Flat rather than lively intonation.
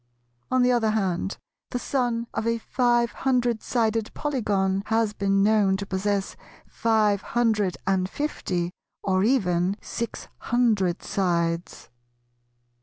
No: average, 3.7 semitones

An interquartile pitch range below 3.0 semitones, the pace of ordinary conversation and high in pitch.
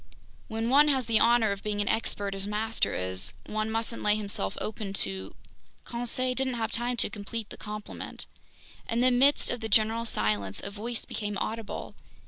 Yes: narrow, 2.6 semitones; average, 180 wpm; high, 220 Hz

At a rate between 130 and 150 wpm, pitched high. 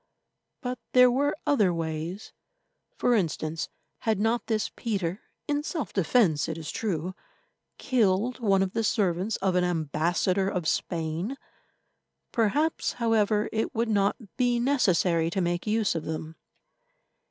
Yes: slow, 135 wpm; high, 200 Hz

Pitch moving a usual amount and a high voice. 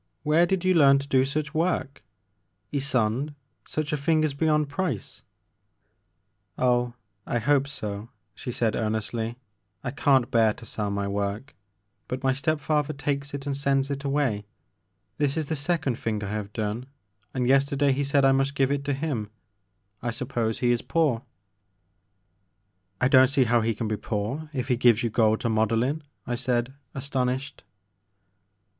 No: average, 3.6 semitones; low, 135 Hz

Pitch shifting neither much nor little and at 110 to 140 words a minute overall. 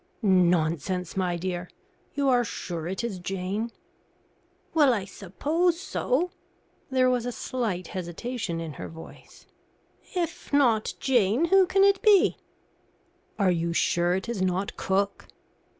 No: wide, 6.4 semitones; slow, 135 wpm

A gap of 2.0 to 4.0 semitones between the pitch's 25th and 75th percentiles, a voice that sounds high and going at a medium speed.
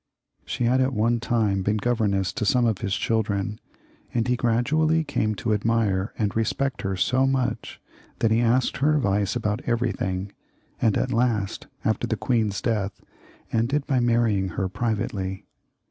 No: average, 3.2 semitones; low, 115 Hz; average, 160 wpm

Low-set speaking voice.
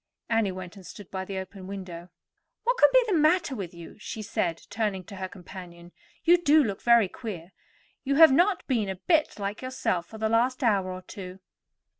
No: high, 205 Hz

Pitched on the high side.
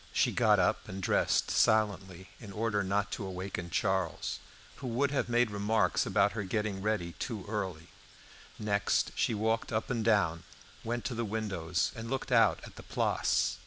No: low, 105 Hz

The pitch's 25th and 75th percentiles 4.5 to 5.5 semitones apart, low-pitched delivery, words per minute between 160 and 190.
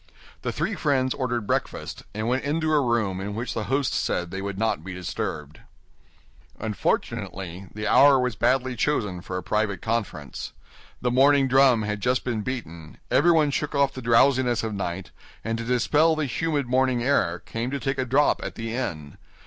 Yes: average, 4.9 semitones; low, 120 Hz; average, 180 wpm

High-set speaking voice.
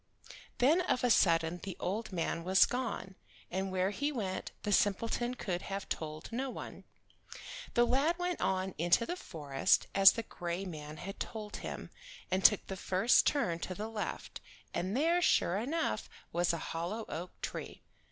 Yes: high, 195 Hz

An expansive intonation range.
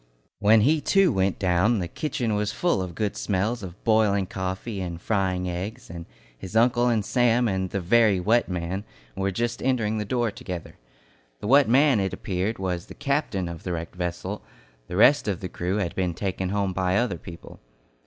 No: average, 4.1 semitones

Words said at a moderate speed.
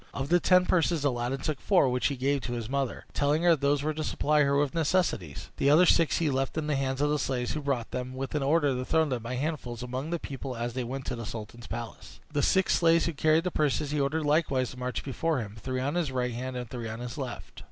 No: fast, 265 wpm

